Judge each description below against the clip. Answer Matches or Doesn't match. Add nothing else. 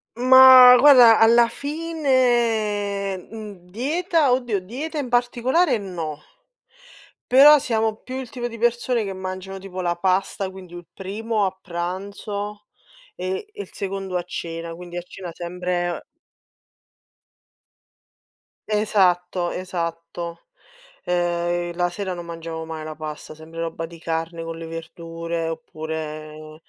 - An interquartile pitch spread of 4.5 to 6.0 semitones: Matches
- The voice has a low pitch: Doesn't match